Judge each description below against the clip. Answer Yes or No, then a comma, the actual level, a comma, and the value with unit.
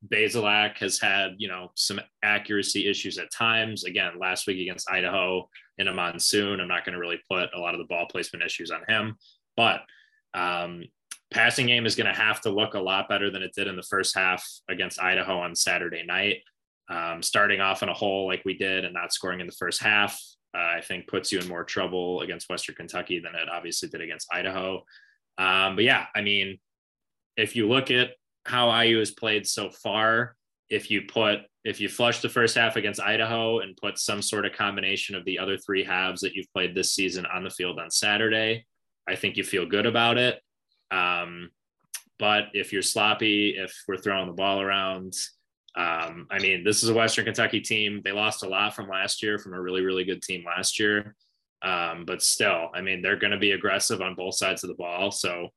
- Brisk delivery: Yes, fast, 215 wpm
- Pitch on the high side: No, low, 100 Hz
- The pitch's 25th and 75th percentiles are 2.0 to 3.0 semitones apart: Yes, narrow, 2.5 semitones